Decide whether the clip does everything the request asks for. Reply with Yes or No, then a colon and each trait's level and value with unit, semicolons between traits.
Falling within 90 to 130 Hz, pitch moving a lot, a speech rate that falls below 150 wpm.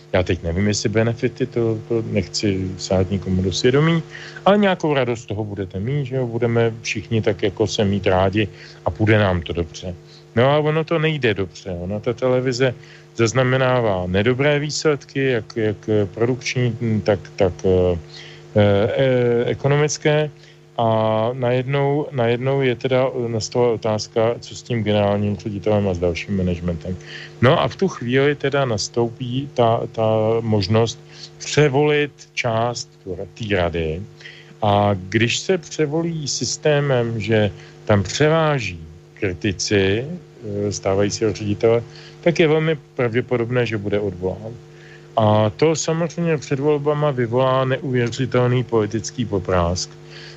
Yes: low, 120 Hz; wide, 5.7 semitones; average, 130 wpm